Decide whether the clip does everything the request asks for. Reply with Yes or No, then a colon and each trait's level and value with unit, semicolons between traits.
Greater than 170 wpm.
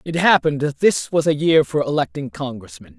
Yes: average, 200 wpm